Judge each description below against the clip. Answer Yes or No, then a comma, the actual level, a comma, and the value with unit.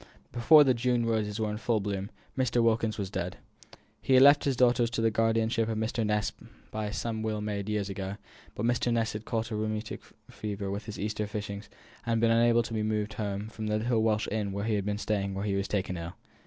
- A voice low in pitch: Yes, low, 110 Hz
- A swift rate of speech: Yes, fast, 230 wpm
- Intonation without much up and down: Yes, narrow, 1.9 semitones